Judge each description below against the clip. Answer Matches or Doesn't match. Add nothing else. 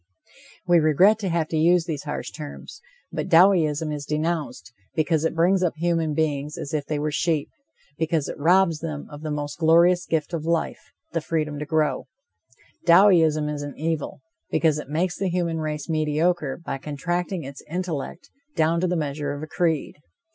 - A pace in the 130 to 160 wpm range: Doesn't match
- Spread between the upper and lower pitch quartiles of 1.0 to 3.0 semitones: Matches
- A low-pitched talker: Doesn't match